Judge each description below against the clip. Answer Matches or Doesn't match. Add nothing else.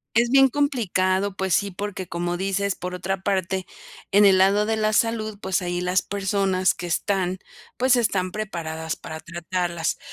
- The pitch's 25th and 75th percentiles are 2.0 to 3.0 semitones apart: Matches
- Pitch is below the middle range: Doesn't match